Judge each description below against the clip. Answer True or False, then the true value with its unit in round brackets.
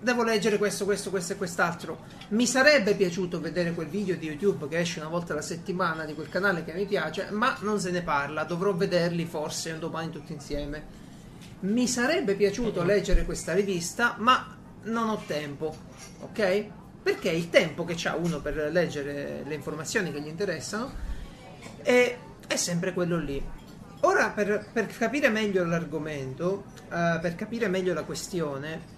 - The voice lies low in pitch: False (180 Hz)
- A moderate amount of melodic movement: True (4.1 semitones)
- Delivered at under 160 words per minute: False (165 wpm)